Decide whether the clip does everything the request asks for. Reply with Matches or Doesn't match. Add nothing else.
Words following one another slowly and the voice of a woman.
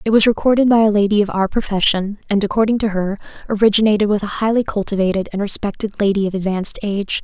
Doesn't match